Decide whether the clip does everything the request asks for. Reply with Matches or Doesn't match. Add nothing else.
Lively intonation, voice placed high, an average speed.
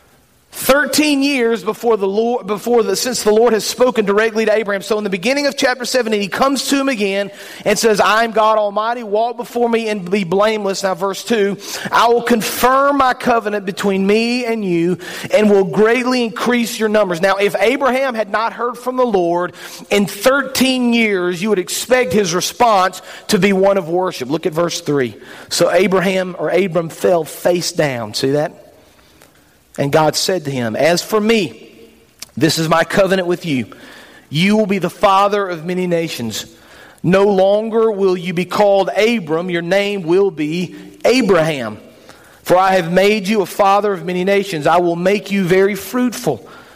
Doesn't match